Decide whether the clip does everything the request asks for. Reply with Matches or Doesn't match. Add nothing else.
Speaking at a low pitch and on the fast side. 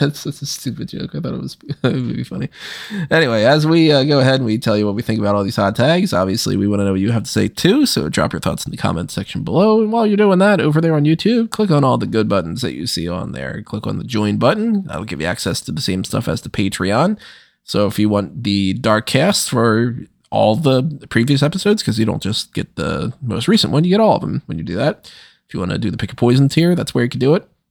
Matches